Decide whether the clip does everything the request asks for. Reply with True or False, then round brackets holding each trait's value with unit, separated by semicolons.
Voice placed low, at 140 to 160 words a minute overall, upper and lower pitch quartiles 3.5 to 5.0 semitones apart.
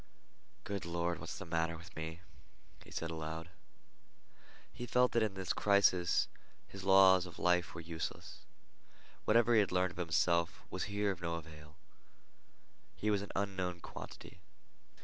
False (90 Hz; 150 wpm; 3.1 semitones)